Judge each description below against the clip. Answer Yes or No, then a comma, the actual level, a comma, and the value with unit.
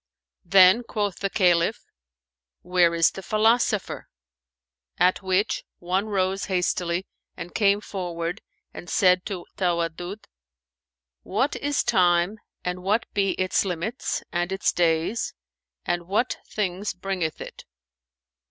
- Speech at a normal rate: No, slow, 115 wpm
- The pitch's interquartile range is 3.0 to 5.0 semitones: No, narrow, 2.6 semitones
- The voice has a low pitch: No, medium, 185 Hz